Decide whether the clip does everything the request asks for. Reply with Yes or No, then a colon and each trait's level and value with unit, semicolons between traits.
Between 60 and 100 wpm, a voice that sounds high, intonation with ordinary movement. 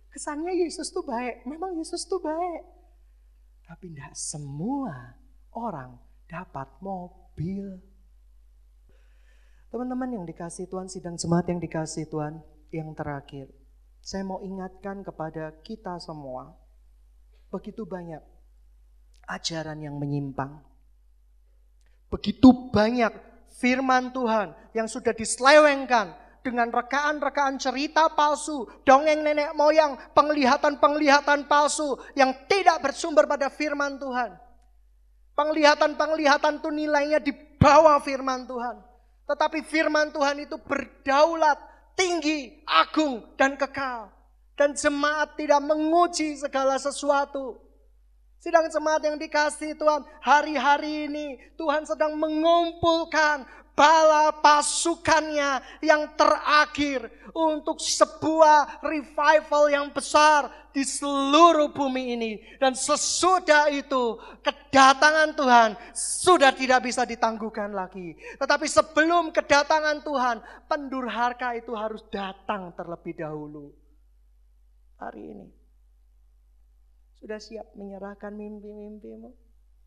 No: average, 95 wpm; very high, 265 Hz; wide, 7.9 semitones